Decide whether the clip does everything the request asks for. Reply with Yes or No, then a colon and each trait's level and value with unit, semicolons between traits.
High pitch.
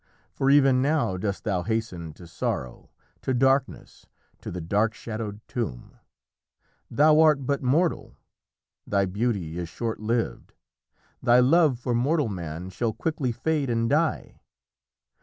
No: low, 120 Hz